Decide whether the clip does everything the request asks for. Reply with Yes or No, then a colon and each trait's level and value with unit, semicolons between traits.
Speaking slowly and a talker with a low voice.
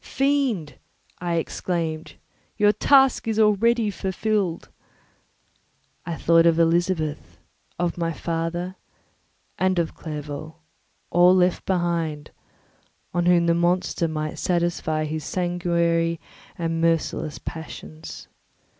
No: slow, 100 wpm; medium, 170 Hz